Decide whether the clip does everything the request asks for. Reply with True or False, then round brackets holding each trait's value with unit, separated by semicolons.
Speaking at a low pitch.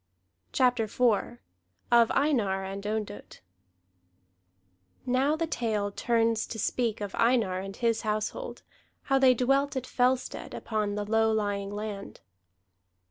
False (225 Hz)